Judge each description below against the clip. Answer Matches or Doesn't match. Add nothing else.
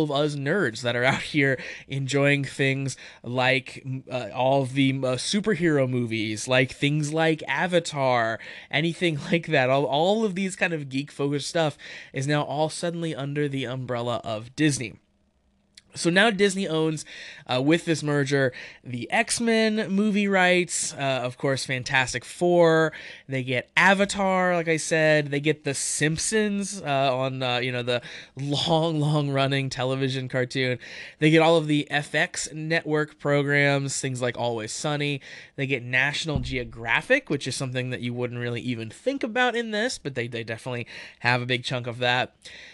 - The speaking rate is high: Doesn't match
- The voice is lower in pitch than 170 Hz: Matches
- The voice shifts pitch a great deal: Doesn't match